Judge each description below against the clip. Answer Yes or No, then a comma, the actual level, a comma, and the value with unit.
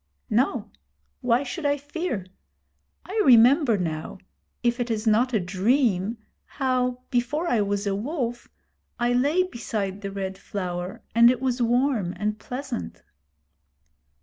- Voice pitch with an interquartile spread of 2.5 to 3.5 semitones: No, average, 4.4 semitones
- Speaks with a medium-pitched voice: No, high, 240 Hz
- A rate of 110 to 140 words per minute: Yes, slow, 135 wpm